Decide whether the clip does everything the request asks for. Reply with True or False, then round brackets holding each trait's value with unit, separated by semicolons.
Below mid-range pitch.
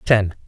True (105 Hz)